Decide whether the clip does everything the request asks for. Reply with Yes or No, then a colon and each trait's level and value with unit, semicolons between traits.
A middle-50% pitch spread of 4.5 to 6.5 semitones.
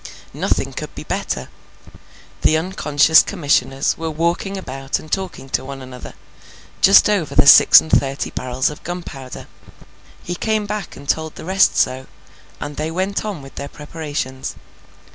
Yes: average, 4.9 semitones